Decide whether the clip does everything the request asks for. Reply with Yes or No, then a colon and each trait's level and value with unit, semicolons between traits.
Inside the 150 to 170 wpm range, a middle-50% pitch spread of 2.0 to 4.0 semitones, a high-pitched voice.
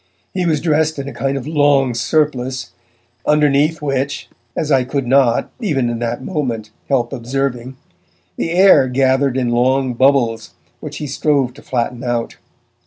No: average, 155 wpm; average, 3.0 semitones; low, 135 Hz